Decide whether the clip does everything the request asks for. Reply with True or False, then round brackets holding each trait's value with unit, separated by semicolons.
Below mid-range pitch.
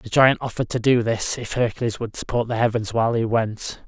True (115 Hz)